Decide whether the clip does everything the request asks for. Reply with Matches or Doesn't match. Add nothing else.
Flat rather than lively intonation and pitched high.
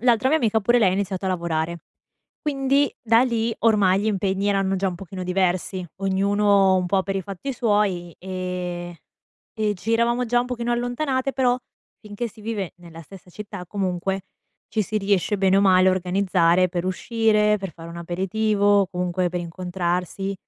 Doesn't match